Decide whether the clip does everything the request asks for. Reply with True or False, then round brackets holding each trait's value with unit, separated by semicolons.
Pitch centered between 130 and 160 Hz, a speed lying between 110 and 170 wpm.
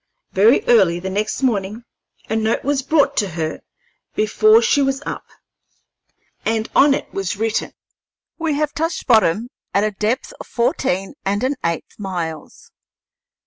False (220 Hz; 145 wpm)